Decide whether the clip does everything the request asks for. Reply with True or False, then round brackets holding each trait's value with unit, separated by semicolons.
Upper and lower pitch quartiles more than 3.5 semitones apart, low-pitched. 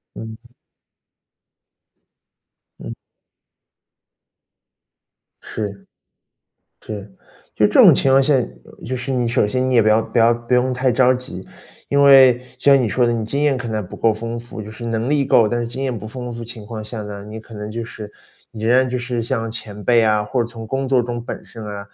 False (2.6 semitones; 120 Hz)